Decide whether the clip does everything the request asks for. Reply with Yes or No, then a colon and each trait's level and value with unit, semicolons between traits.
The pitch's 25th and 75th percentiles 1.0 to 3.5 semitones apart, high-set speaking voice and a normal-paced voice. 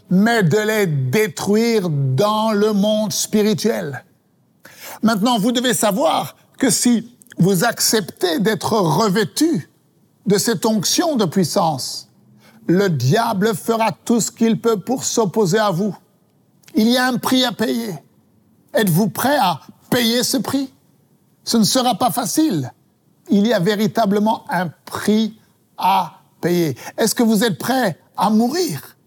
No: narrow, 2.5 semitones; high, 220 Hz; slow, 140 wpm